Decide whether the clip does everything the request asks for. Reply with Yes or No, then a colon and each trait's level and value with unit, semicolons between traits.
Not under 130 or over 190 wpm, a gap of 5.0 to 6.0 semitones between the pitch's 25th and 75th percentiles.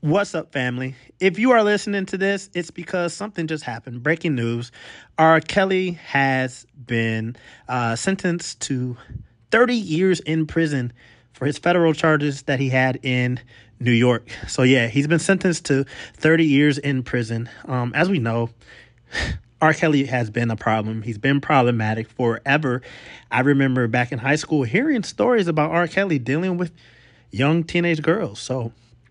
Yes: average, 160 wpm; average, 5.3 semitones